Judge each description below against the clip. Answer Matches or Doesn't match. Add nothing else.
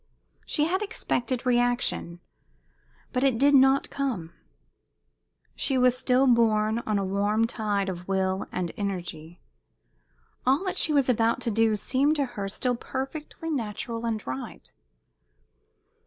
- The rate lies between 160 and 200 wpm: Doesn't match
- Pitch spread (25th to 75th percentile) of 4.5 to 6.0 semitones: Matches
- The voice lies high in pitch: Matches